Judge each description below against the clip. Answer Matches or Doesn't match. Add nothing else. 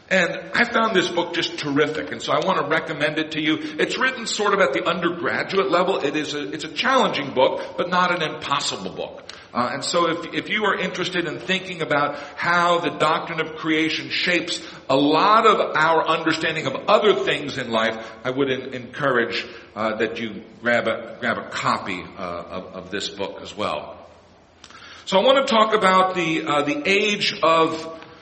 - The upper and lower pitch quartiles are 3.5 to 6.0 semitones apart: Matches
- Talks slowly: Doesn't match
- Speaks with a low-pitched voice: Doesn't match